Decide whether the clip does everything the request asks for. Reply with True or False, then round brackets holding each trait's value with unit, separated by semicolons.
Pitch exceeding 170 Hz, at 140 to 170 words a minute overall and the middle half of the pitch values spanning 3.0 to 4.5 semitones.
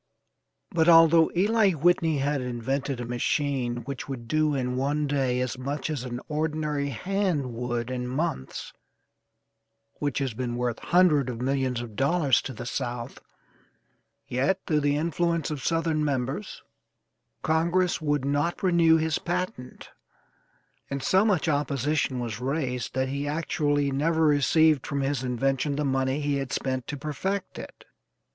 False (140 Hz; 150 wpm; 3.8 semitones)